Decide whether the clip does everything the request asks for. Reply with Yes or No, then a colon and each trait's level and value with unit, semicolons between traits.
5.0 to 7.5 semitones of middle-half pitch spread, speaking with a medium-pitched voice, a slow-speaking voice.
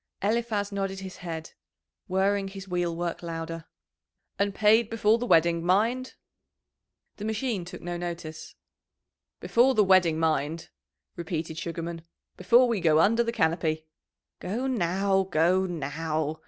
No: average, 3.9 semitones; medium, 180 Hz; slow, 125 wpm